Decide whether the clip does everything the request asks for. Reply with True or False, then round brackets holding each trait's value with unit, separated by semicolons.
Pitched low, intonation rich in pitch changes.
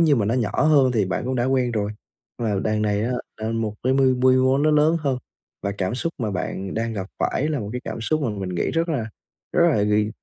False (120 Hz; 4.4 semitones)